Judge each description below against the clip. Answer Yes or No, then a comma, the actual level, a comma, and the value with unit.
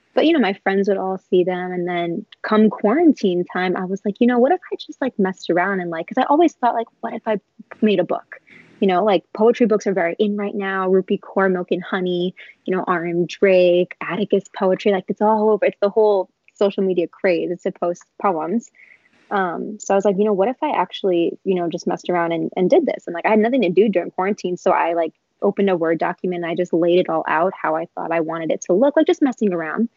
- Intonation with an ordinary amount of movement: Yes, average, 3.4 semitones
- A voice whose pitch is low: No, high, 195 Hz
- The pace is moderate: No, fast, 260 wpm